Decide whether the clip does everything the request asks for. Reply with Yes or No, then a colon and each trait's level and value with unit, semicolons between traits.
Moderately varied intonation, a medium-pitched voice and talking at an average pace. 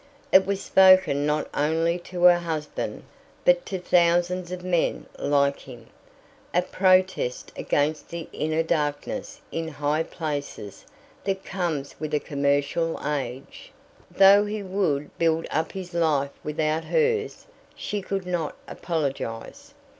No: average, 4.0 semitones; medium, 165 Hz; slow, 130 wpm